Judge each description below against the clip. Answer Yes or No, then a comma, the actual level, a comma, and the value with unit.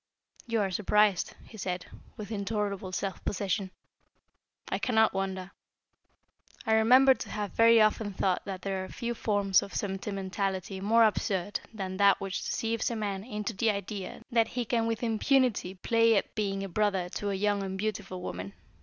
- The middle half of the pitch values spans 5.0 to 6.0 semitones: No, narrow, 2.5 semitones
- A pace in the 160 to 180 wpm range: Yes, average, 170 wpm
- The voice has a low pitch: No, high, 205 Hz